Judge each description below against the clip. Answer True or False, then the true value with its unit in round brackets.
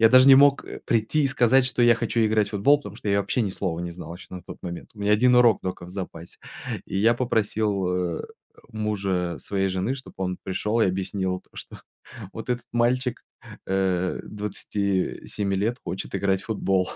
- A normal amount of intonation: True (4.0 semitones)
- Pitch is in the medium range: False (100 Hz)